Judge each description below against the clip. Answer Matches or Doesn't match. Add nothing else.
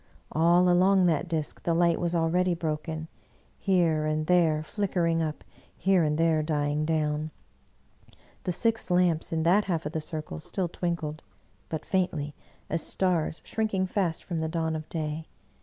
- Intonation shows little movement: Matches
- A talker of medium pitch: Matches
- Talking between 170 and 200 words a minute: Doesn't match